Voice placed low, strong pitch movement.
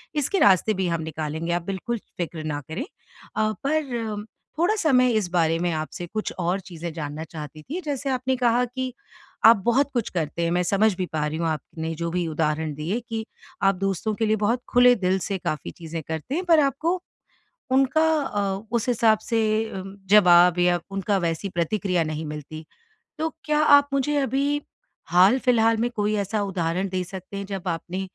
No: high, 195 Hz; wide, 6.3 semitones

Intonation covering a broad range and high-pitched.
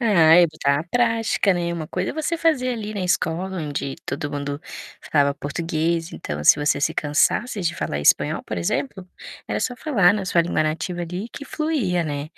No: wide, 6.0 semitones; medium, 170 Hz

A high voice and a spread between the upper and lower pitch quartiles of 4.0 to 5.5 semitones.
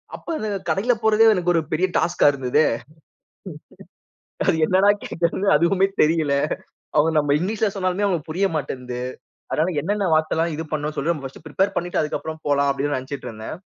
No: medium, 165 Hz; average, 4.5 semitones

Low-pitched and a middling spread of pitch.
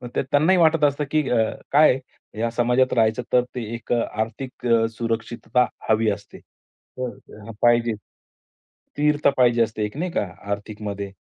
Yes: low, 120 Hz; average, 3.4 semitones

